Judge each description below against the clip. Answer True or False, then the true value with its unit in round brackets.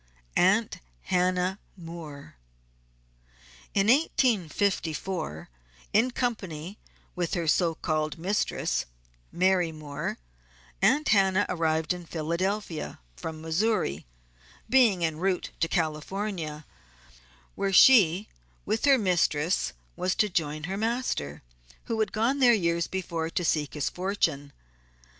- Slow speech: True (110 wpm)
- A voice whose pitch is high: False (180 Hz)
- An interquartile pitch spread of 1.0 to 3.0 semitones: False (4.3 semitones)